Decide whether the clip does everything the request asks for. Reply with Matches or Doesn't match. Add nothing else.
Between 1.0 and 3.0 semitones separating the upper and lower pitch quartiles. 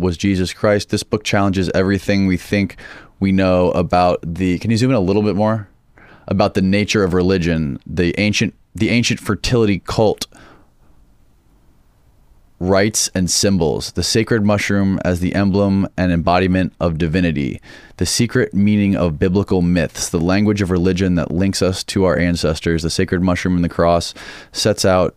Matches